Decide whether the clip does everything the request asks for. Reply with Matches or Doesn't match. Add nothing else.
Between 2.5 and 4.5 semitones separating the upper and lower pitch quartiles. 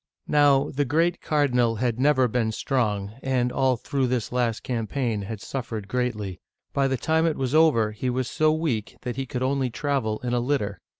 Matches